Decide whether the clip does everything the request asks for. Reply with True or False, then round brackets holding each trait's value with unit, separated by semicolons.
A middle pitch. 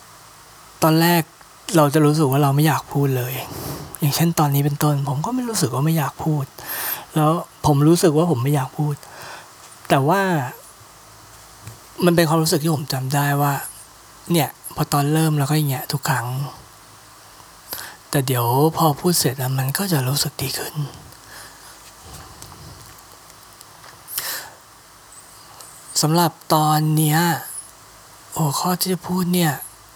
True (150 Hz)